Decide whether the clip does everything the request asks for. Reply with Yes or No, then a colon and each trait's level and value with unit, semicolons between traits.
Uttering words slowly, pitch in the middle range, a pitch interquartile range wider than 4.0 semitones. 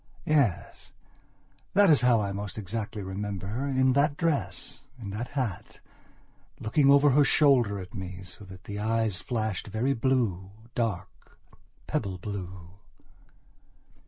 No: slow, 130 wpm; low, 110 Hz; average, 5.2 semitones